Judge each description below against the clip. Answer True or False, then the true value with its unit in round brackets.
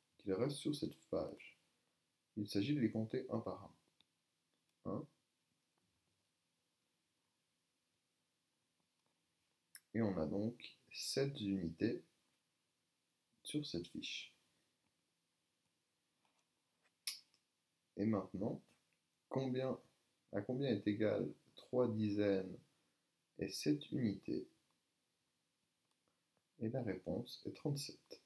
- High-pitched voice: False (105 Hz)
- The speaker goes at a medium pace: False (85 wpm)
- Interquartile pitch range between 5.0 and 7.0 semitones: True (5.3 semitones)